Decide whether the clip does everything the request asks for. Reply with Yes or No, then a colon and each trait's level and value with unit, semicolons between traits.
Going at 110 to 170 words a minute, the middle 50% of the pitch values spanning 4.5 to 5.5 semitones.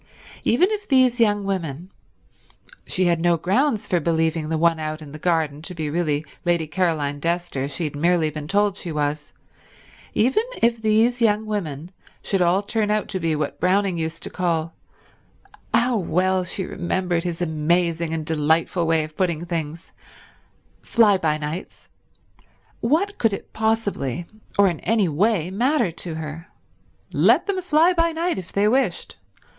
Yes: average, 155 wpm; average, 4.8 semitones